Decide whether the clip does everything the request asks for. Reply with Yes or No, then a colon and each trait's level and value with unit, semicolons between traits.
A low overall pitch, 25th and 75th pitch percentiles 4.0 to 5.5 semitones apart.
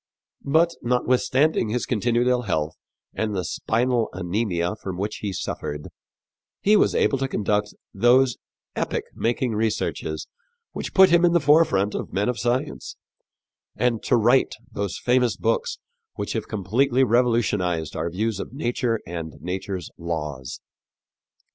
Yes: low, 115 Hz; average, 4.9 semitones